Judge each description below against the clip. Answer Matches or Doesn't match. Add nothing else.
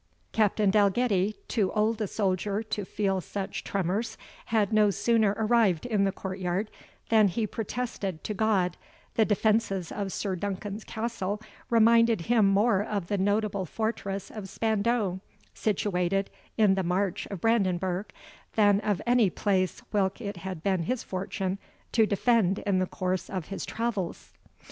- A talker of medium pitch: Doesn't match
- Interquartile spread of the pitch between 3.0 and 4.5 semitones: Doesn't match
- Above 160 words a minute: Doesn't match